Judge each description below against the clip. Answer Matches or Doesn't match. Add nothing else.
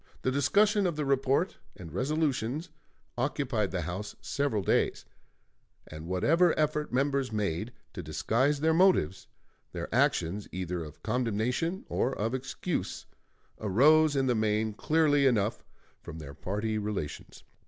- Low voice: Matches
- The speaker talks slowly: Matches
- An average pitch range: Doesn't match